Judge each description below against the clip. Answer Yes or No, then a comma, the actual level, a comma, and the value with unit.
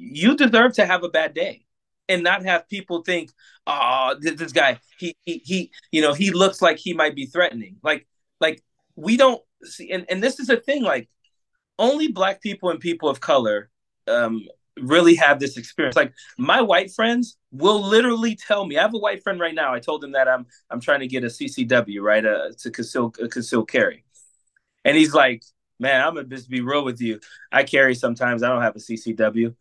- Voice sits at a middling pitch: Yes, medium, 170 Hz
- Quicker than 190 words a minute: Yes, fast, 205 wpm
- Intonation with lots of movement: Yes, wide, 8.4 semitones